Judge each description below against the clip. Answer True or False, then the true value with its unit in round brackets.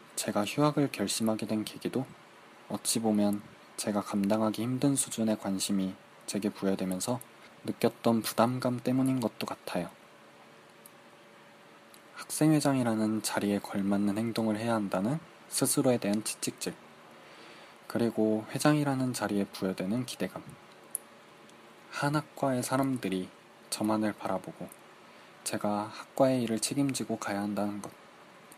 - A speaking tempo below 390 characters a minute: True (275 characters per minute)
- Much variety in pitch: False (3.8 semitones)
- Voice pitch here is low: True (110 Hz)